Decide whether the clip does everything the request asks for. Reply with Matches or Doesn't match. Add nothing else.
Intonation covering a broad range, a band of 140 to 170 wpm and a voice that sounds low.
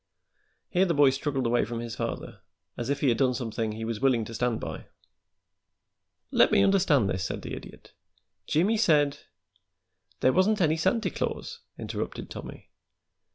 Matches